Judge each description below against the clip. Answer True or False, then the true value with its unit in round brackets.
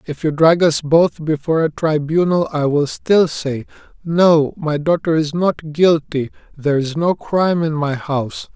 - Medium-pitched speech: True (155 Hz)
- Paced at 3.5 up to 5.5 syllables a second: True (4.4 syllables/s)